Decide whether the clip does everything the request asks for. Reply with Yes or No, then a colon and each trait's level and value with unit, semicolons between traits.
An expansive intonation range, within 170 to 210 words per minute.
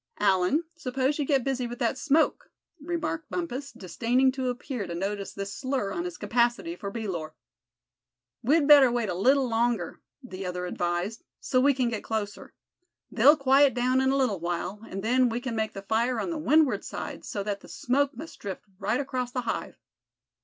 No: average, 5.0 semitones; average, 190 wpm